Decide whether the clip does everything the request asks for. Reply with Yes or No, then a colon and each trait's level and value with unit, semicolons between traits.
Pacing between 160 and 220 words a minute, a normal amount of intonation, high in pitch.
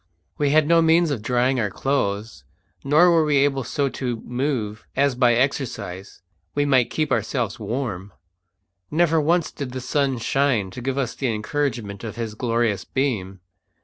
No: average, 165 wpm; average, 4.2 semitones; low, 130 Hz